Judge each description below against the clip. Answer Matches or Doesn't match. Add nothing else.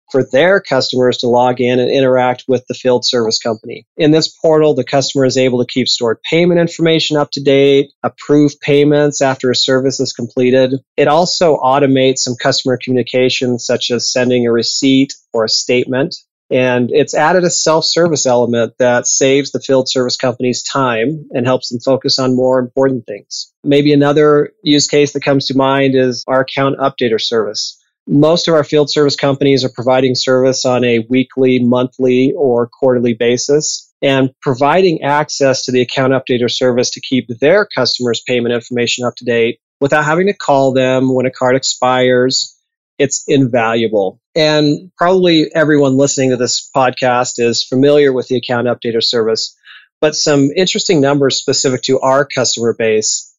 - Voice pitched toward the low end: Matches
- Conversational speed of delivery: Matches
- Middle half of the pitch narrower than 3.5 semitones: Matches